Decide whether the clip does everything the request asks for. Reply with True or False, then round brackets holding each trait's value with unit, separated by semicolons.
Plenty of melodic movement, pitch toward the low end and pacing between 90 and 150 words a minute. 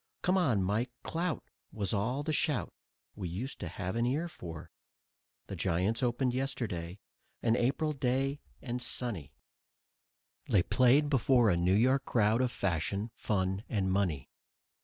True (5.7 semitones; 115 Hz; 145 wpm)